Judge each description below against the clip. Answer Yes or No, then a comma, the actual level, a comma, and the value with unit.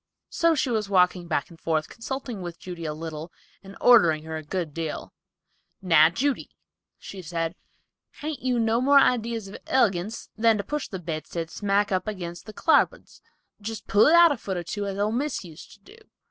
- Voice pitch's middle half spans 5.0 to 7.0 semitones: Yes, wide, 5.5 semitones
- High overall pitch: Yes, high, 195 Hz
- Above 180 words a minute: Yes, average, 195 wpm